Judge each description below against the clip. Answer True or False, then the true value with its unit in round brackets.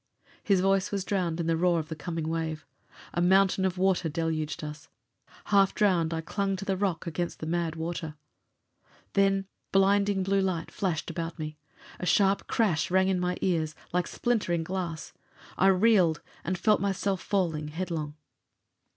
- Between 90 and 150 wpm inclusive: False (165 wpm)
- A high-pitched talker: False (180 Hz)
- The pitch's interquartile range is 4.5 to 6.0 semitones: False (3.1 semitones)